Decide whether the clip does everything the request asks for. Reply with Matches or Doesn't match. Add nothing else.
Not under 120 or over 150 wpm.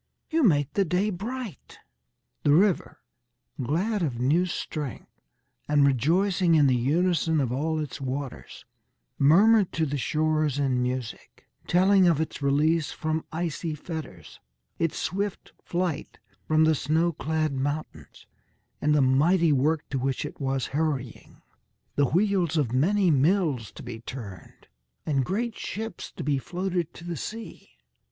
Matches